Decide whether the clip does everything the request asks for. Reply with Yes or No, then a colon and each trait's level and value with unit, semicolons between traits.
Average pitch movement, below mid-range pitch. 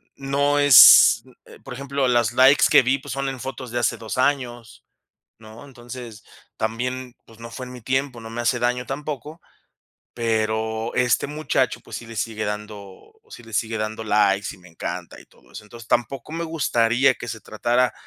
Yes: average, 3.1 semitones; low, 120 Hz